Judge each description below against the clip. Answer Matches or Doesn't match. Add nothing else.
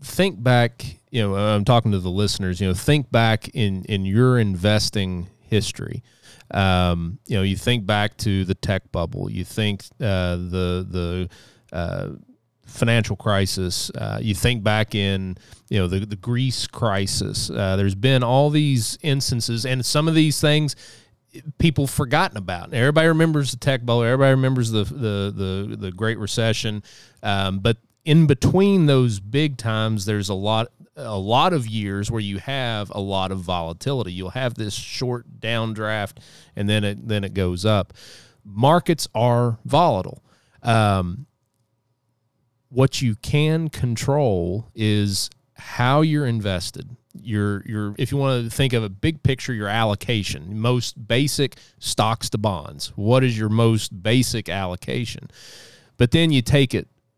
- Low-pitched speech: Matches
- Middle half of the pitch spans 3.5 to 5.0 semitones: Matches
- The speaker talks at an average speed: Matches